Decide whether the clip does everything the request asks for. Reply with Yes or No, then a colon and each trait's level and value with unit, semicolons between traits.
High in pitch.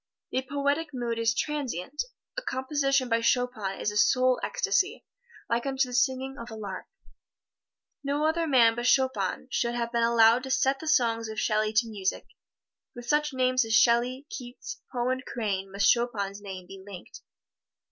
Yes: high, 245 Hz